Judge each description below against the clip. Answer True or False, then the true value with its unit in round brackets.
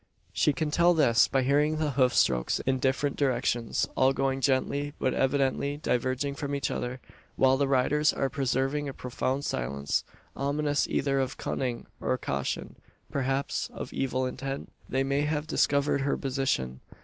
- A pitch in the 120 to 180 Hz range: True (135 Hz)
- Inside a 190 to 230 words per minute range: False (160 wpm)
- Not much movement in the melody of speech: True (1.7 semitones)